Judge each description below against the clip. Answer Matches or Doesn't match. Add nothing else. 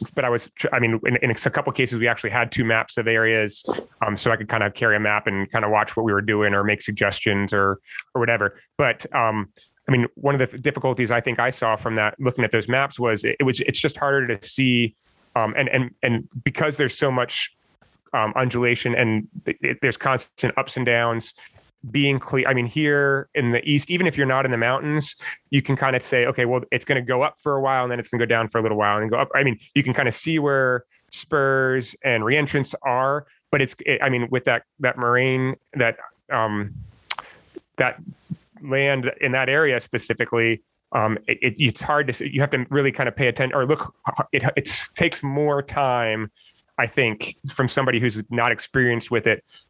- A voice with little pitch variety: Doesn't match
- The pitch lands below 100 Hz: Doesn't match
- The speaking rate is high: Matches